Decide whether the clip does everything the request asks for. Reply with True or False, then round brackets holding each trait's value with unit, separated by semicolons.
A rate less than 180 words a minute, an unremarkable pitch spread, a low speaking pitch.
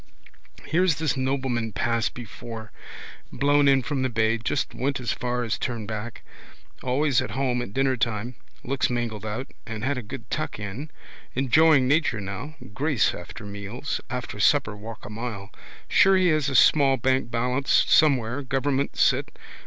True (155 wpm; 3.7 semitones; 125 Hz)